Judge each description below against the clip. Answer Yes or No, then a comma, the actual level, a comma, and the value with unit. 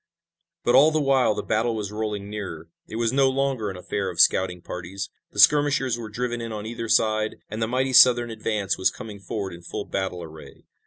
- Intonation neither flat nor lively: Yes, average, 3.8 semitones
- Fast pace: Yes, fast, 210 wpm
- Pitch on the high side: No, low, 110 Hz